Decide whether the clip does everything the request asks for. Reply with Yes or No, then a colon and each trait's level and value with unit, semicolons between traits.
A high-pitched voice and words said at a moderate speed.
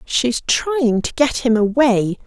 Yes: high, 245 Hz; average, 160 wpm